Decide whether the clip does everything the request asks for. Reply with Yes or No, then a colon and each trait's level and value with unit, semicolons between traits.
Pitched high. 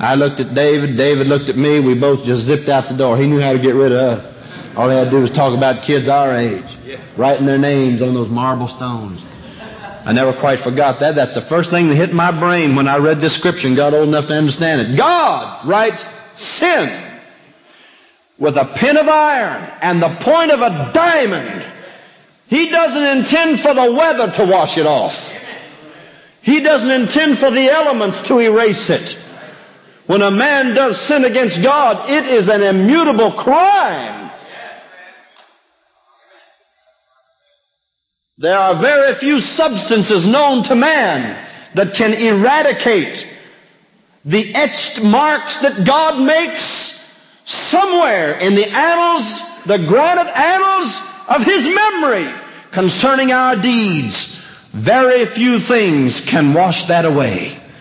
Yes: high, 205 Hz